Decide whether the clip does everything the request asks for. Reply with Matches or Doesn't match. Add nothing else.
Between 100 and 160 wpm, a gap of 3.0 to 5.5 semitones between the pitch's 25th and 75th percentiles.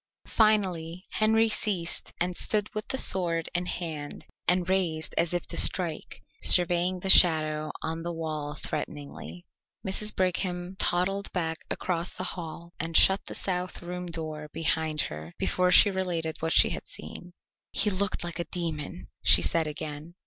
Doesn't match